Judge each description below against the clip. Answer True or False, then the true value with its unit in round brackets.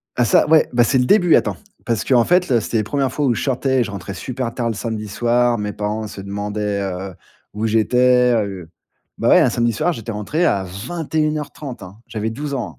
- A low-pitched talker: True (115 Hz)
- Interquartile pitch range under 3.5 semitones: False (4.2 semitones)